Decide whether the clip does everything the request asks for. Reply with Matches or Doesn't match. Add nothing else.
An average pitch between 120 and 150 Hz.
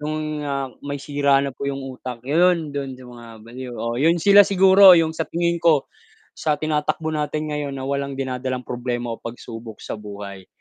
Matches